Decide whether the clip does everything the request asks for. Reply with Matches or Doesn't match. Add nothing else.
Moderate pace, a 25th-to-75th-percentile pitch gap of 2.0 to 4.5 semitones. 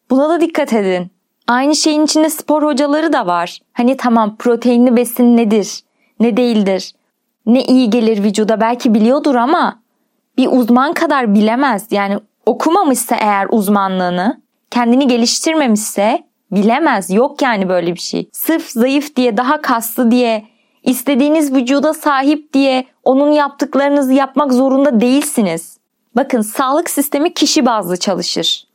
Matches